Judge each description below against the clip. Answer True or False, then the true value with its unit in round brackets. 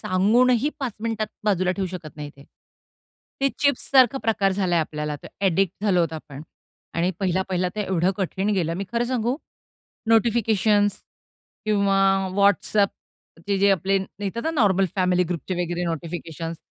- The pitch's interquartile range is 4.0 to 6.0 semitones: False (3.6 semitones)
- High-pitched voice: True (195 Hz)